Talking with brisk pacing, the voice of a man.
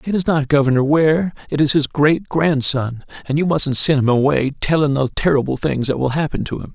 Yes: fast, 220 wpm; male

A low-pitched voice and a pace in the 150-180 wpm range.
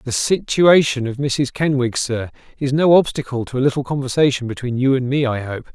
No: low, 130 Hz; average, 200 wpm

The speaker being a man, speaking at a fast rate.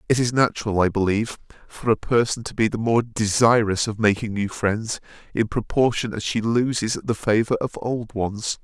No: male; average, 190 wpm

